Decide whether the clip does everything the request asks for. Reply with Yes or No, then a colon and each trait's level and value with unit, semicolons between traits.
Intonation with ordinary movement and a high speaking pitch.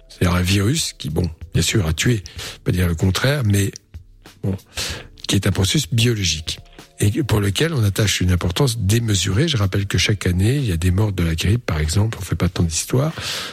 No: average, 4.1 semitones; low, 100 Hz